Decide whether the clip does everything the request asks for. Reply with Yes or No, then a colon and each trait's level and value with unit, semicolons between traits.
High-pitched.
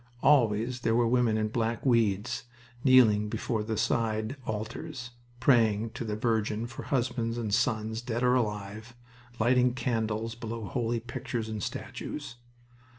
No: low, 115 Hz